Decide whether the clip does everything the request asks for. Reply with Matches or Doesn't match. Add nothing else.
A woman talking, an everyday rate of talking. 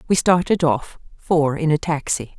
Matches